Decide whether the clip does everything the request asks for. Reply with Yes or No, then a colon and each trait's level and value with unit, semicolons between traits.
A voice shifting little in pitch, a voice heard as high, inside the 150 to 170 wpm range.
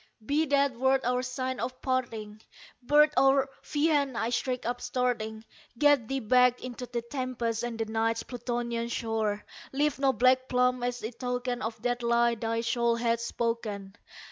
Yes: narrow, 1.9 semitones; high, 245 Hz; average, 160 wpm